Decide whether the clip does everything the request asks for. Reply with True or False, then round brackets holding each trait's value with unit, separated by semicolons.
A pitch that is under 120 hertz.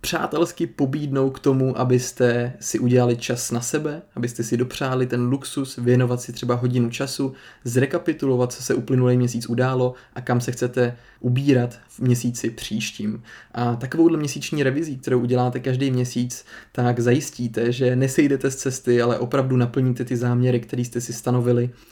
False (125 Hz)